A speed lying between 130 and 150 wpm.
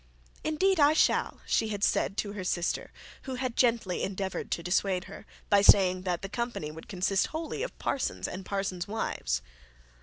No: average, 170 wpm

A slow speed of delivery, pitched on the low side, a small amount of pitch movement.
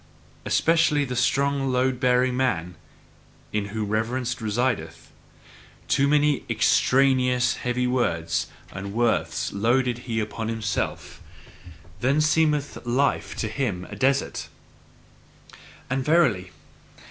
No: slow, 105 wpm; low, 125 Hz; average, 3.6 semitones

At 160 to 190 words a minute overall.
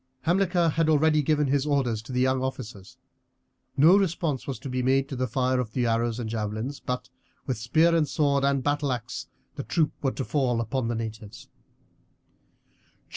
Yes: average, 175 wpm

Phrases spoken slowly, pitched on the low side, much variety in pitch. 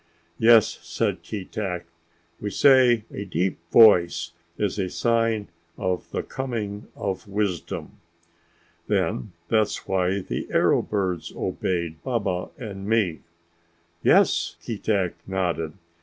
No: slow, 110 wpm; low, 100 Hz; average, 3.4 semitones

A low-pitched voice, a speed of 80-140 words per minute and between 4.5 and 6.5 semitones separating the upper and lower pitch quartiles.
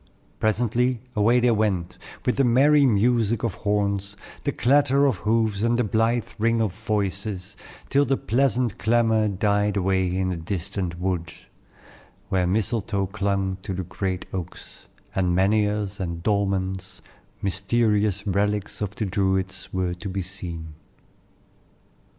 No: low, 100 Hz; slow, 135 wpm; average, 3.0 semitones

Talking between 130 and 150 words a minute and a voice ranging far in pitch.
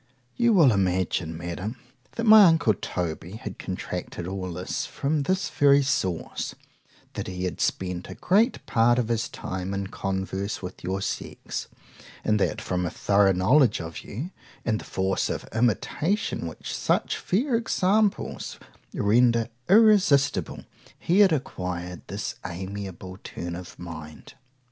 Yes: average, 140 wpm; wide, 7.9 semitones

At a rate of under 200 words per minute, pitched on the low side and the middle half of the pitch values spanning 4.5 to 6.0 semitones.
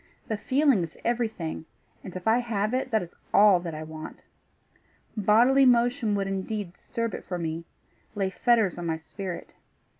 No: average, 170 wpm; high, 205 Hz; average, 5.0 semitones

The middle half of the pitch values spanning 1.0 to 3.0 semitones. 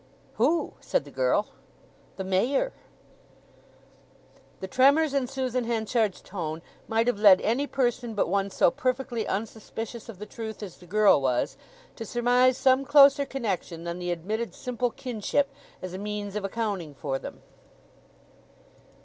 No: average, 4.7 semitones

